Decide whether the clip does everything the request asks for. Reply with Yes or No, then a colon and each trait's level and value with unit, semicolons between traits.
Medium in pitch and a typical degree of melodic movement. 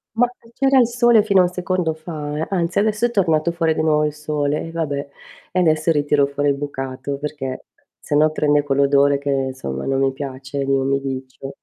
Yes: medium, 150 Hz; average, 3.4 semitones